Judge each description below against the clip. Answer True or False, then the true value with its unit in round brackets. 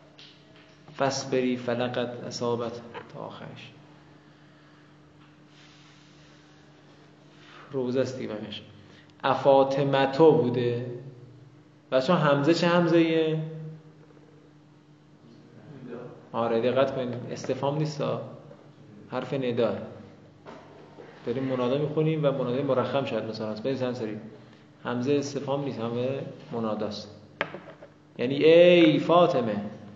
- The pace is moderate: False (80 wpm)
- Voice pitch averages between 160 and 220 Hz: False (135 Hz)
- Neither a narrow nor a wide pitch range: True (3.7 semitones)